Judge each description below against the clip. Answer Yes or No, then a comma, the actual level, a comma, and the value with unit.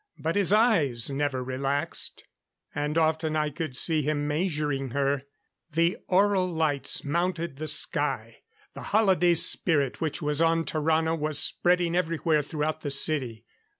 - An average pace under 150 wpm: Yes, average, 140 wpm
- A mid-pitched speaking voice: Yes, medium, 155 Hz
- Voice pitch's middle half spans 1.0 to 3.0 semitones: Yes, narrow, 2.6 semitones